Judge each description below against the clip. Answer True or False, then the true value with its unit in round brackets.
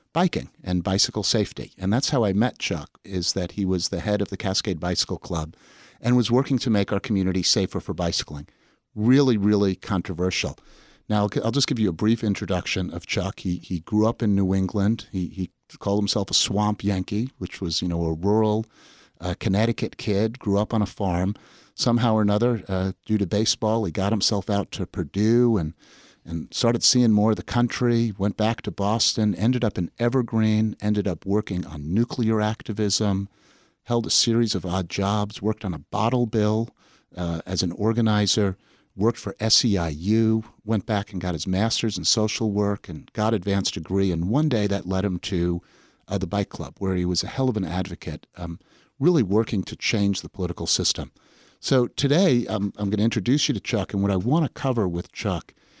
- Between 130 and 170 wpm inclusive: False (195 wpm)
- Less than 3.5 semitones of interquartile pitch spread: True (3.1 semitones)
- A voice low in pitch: True (105 Hz)